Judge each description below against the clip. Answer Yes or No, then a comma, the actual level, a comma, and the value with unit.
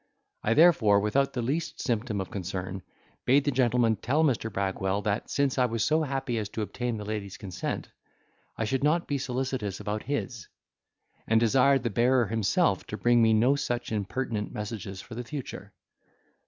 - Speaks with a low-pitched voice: Yes, low, 115 Hz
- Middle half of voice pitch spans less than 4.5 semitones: Yes, average, 4.0 semitones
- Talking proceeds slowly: No, average, 175 wpm